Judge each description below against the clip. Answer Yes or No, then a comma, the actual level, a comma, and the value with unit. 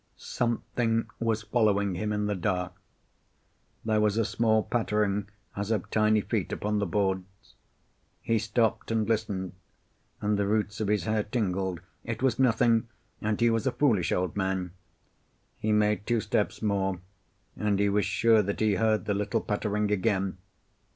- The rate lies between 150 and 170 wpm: Yes, average, 160 wpm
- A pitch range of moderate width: No, narrow, 1.8 semitones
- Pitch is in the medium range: No, low, 105 Hz